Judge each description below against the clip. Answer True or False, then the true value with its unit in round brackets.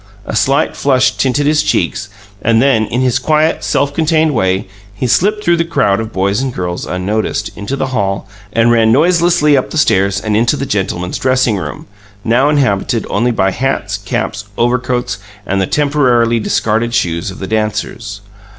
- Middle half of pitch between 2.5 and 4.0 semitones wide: False (5.3 semitones)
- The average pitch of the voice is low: True (120 Hz)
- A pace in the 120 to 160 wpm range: False (175 wpm)